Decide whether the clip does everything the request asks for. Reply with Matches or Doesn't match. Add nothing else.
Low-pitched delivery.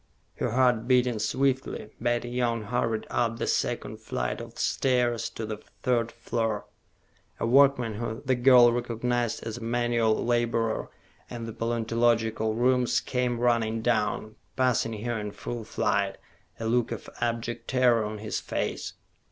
Matches